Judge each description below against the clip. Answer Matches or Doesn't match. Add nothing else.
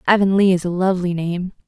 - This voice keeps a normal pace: Matches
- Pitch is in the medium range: Matches